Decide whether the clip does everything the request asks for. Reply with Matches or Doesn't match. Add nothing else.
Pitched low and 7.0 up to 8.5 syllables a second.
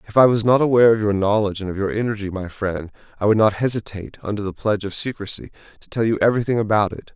Matches